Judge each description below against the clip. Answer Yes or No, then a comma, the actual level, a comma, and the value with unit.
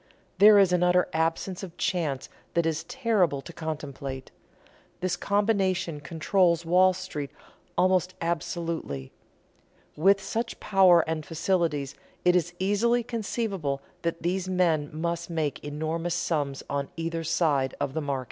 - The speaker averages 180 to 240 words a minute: No, slow, 135 wpm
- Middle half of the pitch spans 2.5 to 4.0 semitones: Yes, average, 3.2 semitones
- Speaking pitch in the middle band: Yes, medium, 170 Hz